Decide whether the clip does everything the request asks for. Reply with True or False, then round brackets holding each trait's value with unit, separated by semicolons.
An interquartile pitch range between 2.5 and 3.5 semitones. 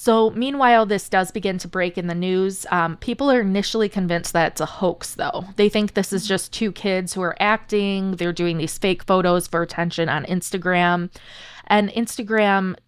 True (3.0 semitones)